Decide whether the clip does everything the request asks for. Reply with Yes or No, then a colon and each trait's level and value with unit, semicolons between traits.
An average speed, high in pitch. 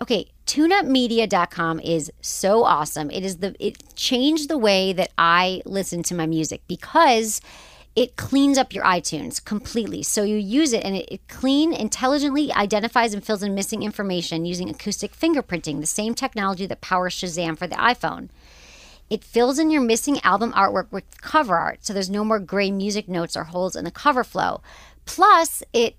Yes: average, 180 wpm; high, 205 Hz